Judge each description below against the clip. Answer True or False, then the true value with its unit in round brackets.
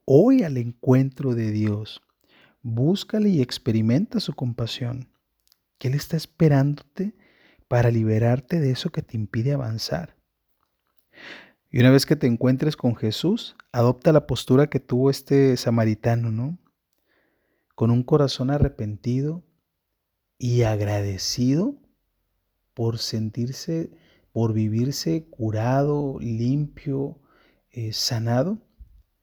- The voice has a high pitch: False (125 Hz)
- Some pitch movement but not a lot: True (4.2 semitones)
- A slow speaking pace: True (105 wpm)